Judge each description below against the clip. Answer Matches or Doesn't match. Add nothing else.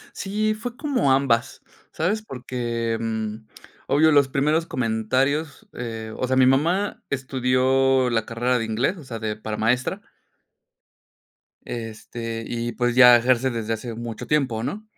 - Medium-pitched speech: Doesn't match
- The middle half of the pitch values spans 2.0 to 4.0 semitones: Matches